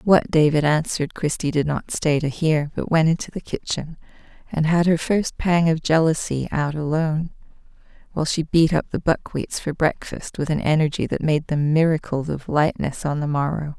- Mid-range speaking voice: Yes, medium, 155 Hz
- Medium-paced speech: Yes, average, 185 wpm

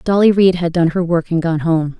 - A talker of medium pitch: Yes, medium, 170 Hz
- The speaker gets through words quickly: Yes, fast, 270 wpm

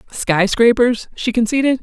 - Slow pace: Yes, slow, 130 wpm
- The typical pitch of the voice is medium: No, high, 235 Hz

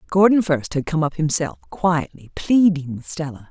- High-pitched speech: No, medium, 155 Hz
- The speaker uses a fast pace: No, average, 170 wpm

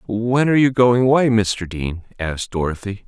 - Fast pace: No, average, 175 wpm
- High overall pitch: No, low, 110 Hz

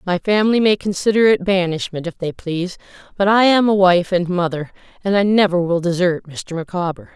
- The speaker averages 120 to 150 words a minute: No, average, 195 wpm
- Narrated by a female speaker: Yes, female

